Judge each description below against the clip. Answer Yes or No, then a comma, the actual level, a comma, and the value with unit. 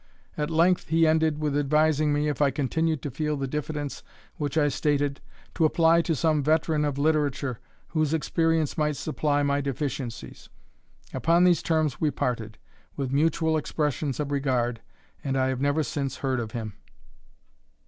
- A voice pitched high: No, medium, 150 Hz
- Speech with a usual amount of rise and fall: No, narrow, 2.3 semitones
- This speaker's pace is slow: No, average, 160 wpm